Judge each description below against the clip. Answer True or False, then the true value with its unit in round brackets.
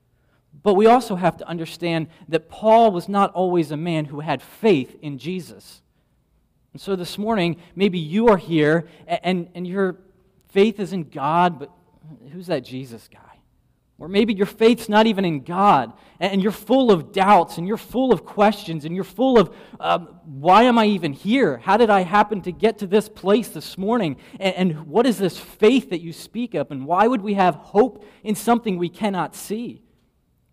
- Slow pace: False (190 wpm)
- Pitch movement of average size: True (4.5 semitones)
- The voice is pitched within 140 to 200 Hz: True (190 Hz)